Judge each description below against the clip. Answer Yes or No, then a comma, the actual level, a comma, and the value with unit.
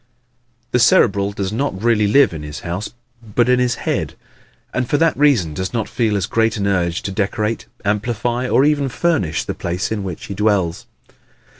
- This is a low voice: Yes, low, 105 Hz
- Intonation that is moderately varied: Yes, average, 4.4 semitones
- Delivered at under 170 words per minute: No, average, 185 wpm